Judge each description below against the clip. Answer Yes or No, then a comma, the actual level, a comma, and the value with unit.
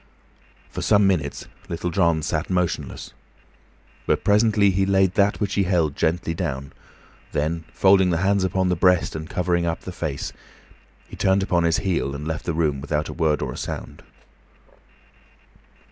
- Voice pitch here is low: Yes, very low, 90 Hz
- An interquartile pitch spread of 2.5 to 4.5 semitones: Yes, average, 3.1 semitones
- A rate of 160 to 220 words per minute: Yes, average, 165 wpm